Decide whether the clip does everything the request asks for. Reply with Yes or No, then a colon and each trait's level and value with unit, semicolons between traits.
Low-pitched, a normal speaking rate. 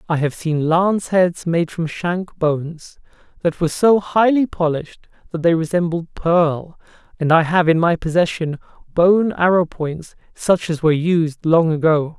No: medium, 170 Hz; average, 165 wpm